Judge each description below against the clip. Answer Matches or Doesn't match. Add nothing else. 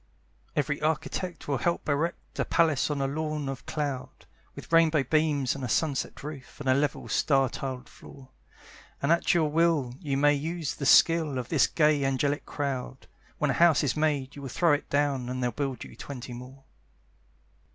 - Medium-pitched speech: Matches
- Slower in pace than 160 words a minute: Doesn't match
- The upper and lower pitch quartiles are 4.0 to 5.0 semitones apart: Doesn't match